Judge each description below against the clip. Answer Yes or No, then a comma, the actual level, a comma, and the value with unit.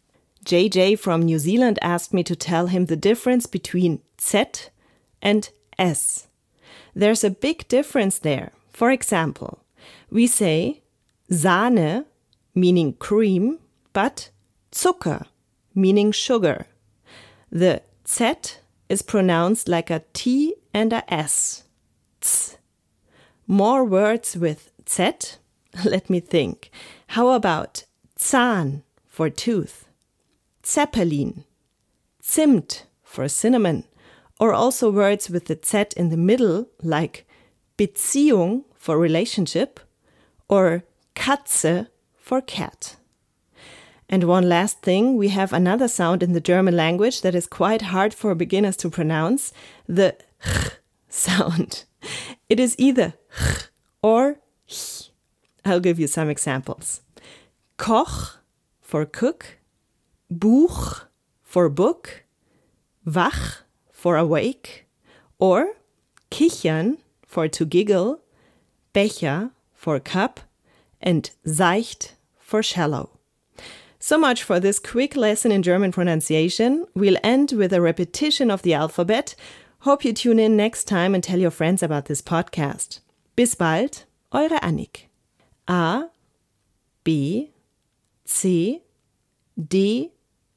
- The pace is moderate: No, slow, 110 wpm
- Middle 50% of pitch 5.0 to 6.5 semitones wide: Yes, wide, 5.5 semitones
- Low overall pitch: No, high, 190 Hz